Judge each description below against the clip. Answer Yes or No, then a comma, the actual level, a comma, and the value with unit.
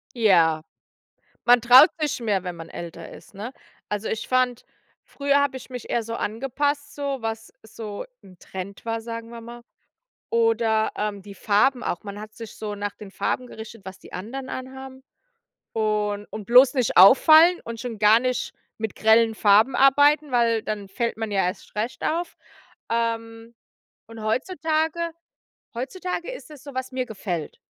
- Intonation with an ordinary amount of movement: Yes, average, 3.7 semitones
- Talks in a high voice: Yes, high, 230 Hz